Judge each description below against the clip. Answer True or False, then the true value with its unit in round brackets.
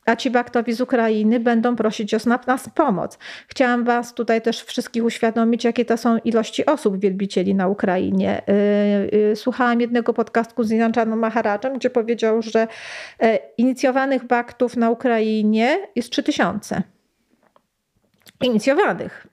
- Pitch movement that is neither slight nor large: False (1.8 semitones)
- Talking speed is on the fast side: False (125 wpm)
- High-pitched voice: True (230 Hz)